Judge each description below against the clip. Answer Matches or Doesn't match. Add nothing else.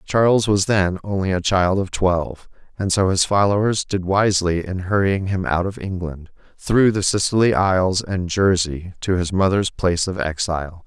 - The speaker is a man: Matches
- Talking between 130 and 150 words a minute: Doesn't match